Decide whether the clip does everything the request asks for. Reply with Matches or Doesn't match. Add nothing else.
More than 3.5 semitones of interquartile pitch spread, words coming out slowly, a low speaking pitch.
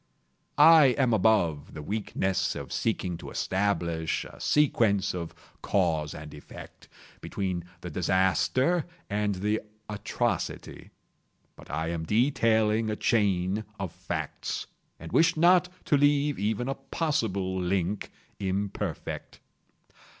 Matches